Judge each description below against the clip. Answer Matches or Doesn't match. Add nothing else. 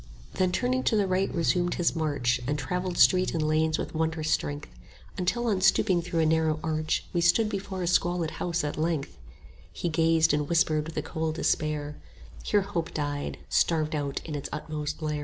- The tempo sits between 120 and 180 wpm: Doesn't match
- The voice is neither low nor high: Matches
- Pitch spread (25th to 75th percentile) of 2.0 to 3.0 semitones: Matches